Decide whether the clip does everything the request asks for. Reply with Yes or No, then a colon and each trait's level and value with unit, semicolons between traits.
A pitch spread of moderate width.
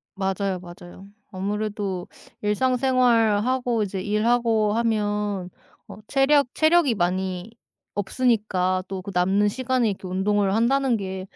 Yes: average, 3.8 semitones